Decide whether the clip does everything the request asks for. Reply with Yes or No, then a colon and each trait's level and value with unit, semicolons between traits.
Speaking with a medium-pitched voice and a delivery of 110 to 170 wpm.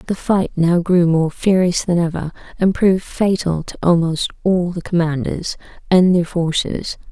Yes: medium, 175 Hz; average, 160 wpm